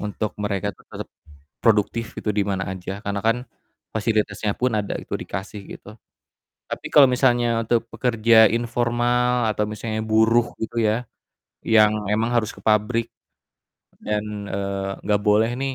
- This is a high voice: No, low, 110 Hz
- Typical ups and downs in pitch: No, narrow, 2.2 semitones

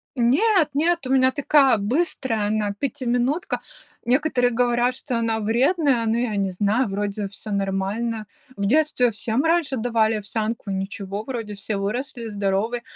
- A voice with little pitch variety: No, average, 4.1 semitones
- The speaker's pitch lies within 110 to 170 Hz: No, high, 230 Hz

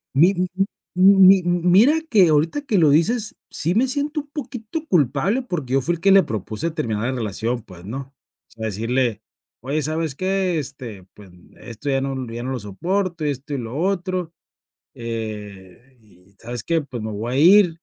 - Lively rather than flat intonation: Yes, wide, 8.1 semitones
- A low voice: No, medium, 145 Hz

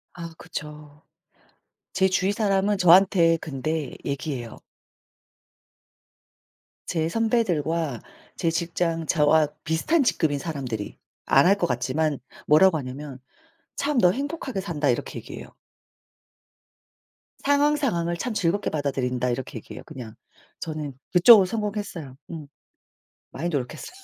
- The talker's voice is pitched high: No, medium, 165 Hz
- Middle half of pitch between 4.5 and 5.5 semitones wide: Yes, average, 5.2 semitones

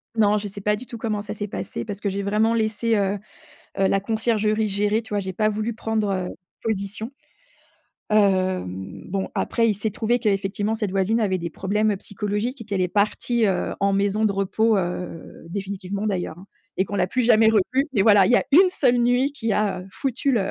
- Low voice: No, high, 210 Hz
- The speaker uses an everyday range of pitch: No, narrow, 2.3 semitones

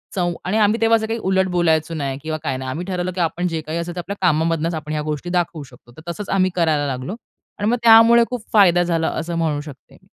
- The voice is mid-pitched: Yes, medium, 170 Hz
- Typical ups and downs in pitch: Yes, average, 3.5 semitones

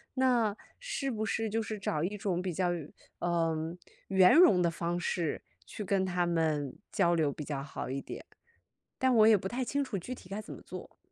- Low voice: No, medium, 185 Hz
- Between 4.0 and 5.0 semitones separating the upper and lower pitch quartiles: Yes, average, 4.7 semitones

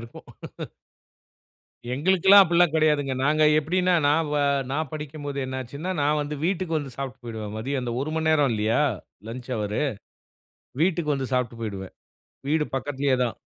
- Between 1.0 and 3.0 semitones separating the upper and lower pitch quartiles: No, average, 3.8 semitones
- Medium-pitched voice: Yes, medium, 145 Hz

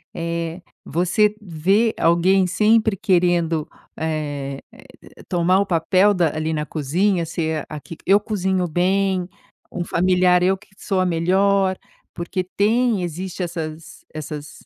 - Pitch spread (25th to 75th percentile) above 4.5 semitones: No, average, 2.8 semitones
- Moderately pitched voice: Yes, medium, 180 Hz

